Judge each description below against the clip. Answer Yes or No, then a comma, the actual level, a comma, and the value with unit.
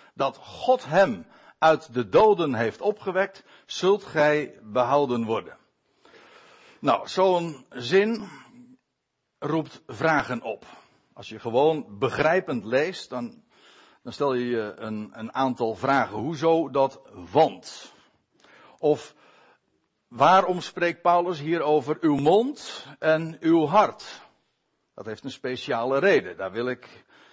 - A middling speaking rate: No, slow, 120 wpm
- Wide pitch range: Yes, wide, 7.1 semitones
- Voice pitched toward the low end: No, medium, 155 Hz